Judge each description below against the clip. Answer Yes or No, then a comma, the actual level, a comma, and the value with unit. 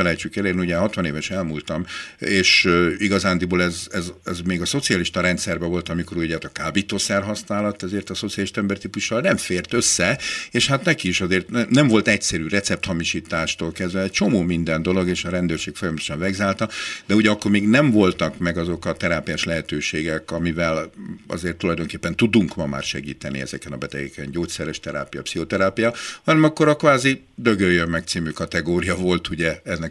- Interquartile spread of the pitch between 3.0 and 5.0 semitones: Yes, average, 3.6 semitones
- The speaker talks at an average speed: No, fast, 165 wpm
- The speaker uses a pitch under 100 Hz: Yes, very low, 90 Hz